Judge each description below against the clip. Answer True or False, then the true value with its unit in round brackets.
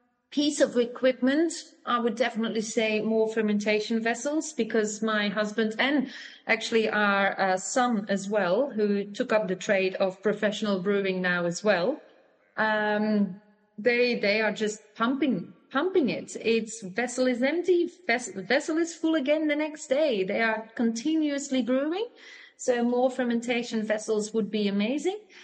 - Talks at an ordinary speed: True (145 wpm)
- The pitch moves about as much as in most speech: True (4.3 semitones)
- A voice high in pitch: True (230 Hz)